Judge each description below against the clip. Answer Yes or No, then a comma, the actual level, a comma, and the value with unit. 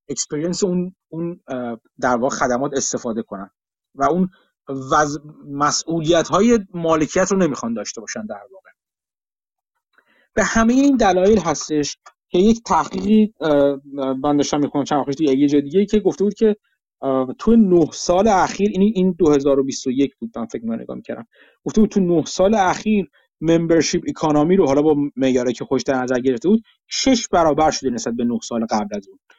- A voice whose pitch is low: No, medium, 155 Hz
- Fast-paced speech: Yes, fast, 165 wpm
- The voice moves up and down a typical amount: No, wide, 6.0 semitones